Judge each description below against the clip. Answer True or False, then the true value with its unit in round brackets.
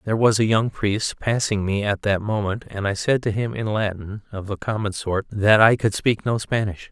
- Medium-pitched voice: False (105 Hz)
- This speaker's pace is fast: True (235 wpm)